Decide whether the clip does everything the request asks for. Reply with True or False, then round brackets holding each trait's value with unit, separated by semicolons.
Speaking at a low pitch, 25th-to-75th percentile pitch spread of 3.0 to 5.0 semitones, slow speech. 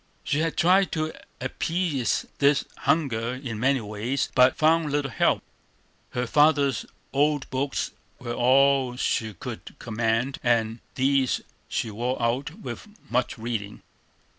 True (130 Hz; 3.7 semitones; 130 wpm)